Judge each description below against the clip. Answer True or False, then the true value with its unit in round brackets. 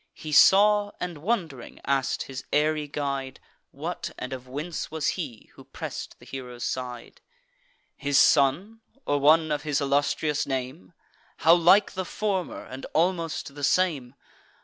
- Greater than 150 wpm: False (145 wpm)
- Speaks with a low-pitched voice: False (145 Hz)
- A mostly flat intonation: False (4.2 semitones)